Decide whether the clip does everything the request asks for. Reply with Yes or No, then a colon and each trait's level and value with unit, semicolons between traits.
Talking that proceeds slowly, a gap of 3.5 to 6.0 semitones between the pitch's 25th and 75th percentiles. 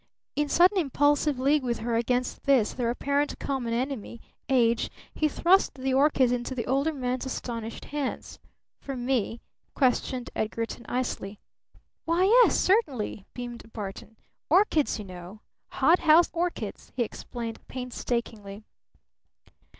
Yes: slow, 125 wpm; average, 3.9 semitones